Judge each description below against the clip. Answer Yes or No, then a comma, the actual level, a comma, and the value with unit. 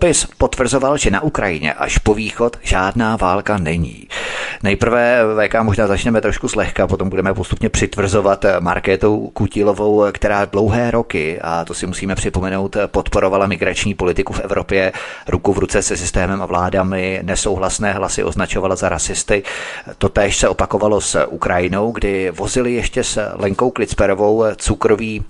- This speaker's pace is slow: No, average, 140 wpm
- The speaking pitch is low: Yes, low, 100 Hz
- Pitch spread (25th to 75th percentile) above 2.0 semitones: Yes, narrow, 2.5 semitones